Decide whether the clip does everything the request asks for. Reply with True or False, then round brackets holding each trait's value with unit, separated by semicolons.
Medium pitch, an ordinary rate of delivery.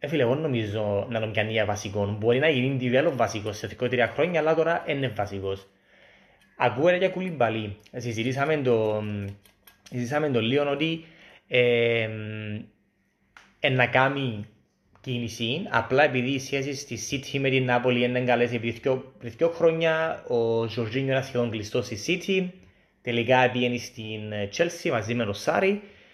False (120 Hz; 160 wpm)